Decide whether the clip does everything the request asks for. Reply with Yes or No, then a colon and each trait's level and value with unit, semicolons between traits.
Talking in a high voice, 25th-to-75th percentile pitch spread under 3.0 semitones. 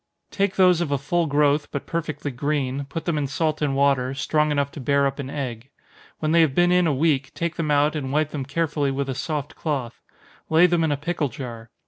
No: medium, 145 Hz; narrow, 2.6 semitones